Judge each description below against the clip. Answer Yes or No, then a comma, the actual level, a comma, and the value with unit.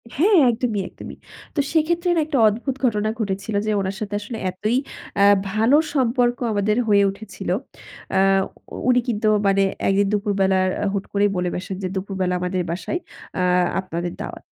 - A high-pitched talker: Yes, high, 210 Hz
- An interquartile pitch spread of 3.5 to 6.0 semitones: Yes, average, 4.0 semitones